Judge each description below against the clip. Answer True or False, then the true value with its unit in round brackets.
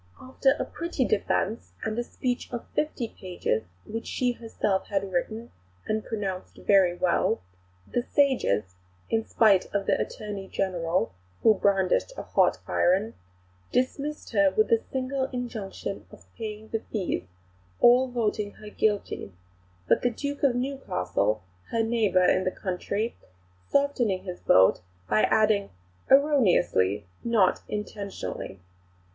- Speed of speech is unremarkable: False (130 wpm)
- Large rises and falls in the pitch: False (4.9 semitones)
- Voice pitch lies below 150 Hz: False (215 Hz)